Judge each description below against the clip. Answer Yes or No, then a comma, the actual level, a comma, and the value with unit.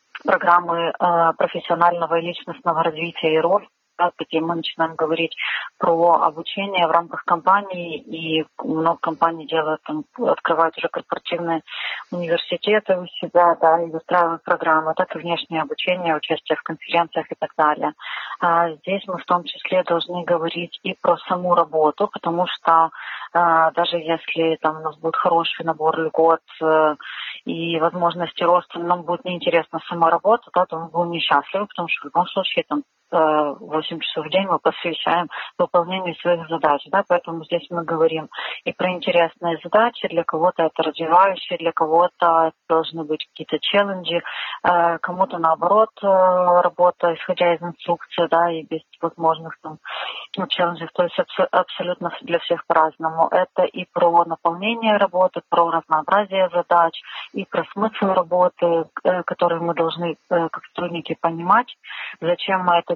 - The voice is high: No, medium, 170 Hz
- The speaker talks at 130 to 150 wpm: Yes, average, 145 wpm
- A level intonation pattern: Yes, narrow, 1.4 semitones